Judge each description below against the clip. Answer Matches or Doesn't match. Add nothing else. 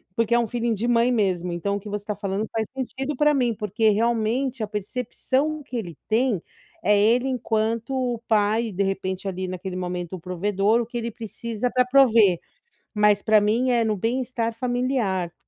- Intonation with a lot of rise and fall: Doesn't match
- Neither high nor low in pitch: Doesn't match